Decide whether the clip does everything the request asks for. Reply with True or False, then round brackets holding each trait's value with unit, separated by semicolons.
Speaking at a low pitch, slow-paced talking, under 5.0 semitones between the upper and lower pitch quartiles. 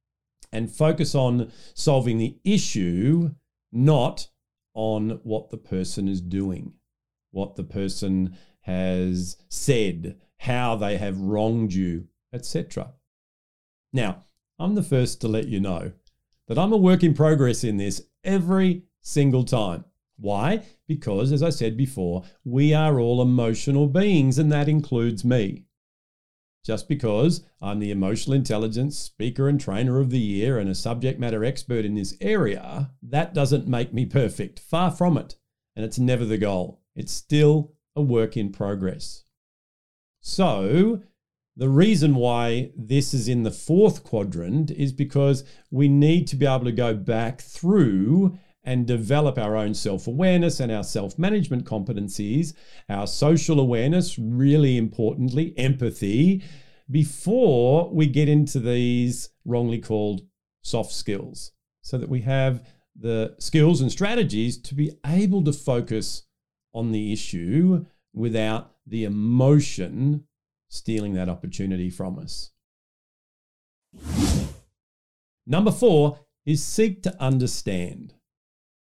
False (125 Hz; 130 wpm; 5.6 semitones)